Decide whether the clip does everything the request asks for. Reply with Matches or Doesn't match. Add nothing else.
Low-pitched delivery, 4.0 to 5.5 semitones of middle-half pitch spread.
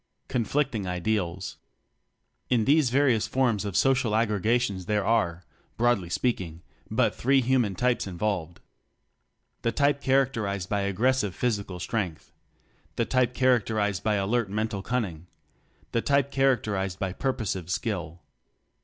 Matches